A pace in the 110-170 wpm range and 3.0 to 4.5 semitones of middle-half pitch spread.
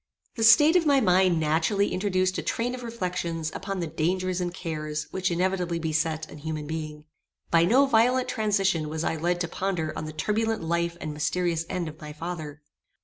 No: average, 190 wpm; average, 3.8 semitones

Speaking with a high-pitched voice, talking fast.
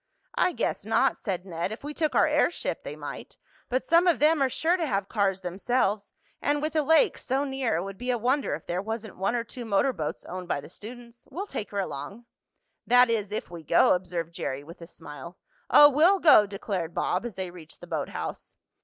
Yes: high, 215 Hz; fast, 220 wpm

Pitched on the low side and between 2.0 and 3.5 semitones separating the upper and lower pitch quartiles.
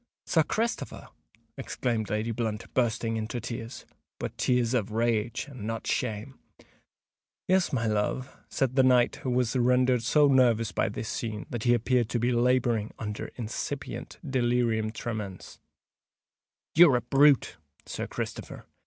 Yes: low, 120 Hz; narrow, 2.4 semitones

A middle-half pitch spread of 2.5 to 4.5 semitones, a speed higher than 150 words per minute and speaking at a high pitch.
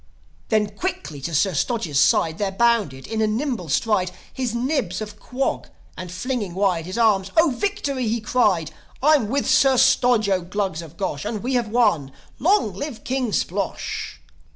No: wide, 5.4 semitones; average, 170 wpm; high, 215 Hz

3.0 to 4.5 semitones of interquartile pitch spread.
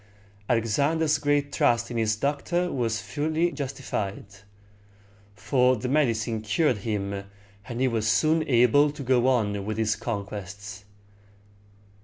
No: average, 4.9 semitones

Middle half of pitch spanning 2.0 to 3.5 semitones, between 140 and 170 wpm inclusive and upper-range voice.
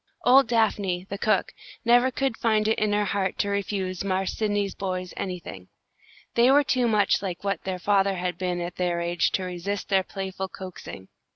No: narrow, 2.6 semitones; average, 185 wpm; high, 195 Hz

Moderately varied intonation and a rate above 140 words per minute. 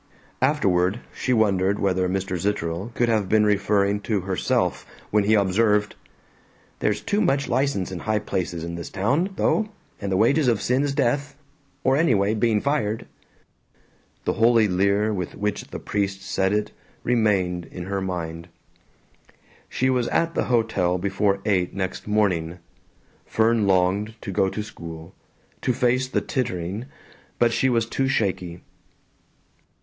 Yes: average, 3.8 semitones; average, 150 wpm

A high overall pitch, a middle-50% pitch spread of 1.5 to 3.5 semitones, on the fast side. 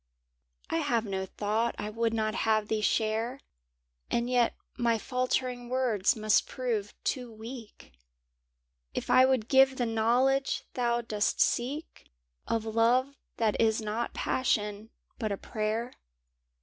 No: high, 230 Hz; narrow, 2.5 semitones; slow, 135 wpm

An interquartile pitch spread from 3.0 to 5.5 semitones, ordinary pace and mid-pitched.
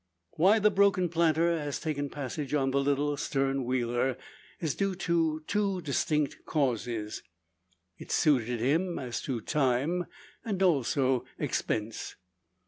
No: average, 4.7 semitones; slow, 130 wpm; medium, 145 Hz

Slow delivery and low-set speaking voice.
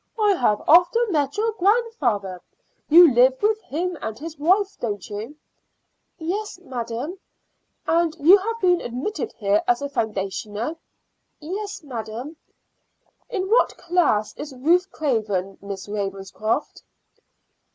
No: slow, 120 wpm; very high, 295 Hz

